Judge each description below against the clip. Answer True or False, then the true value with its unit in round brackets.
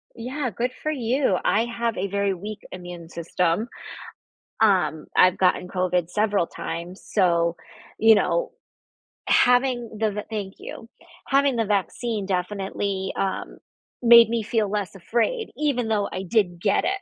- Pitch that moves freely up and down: False (4.3 semitones)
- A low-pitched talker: False (210 Hz)